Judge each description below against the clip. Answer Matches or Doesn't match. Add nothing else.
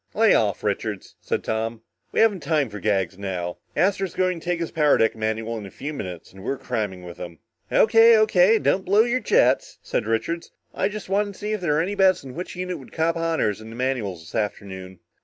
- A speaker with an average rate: Doesn't match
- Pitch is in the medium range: Matches